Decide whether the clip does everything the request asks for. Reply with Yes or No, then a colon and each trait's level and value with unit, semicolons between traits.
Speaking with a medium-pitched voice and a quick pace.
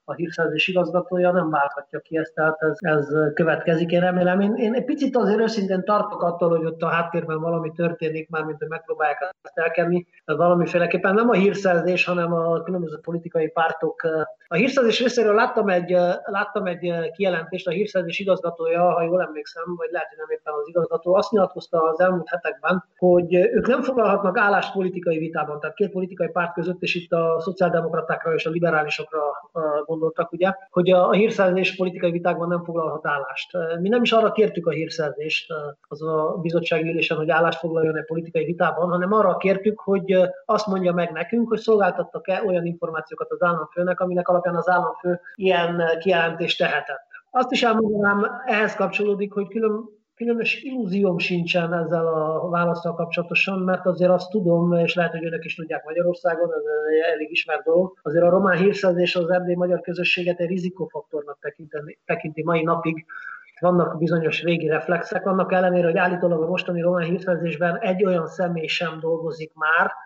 Yes: medium, 175 Hz; fast, 170 wpm